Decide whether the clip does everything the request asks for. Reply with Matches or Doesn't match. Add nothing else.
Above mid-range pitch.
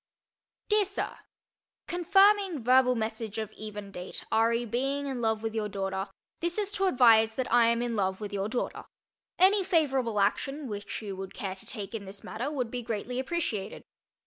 Matches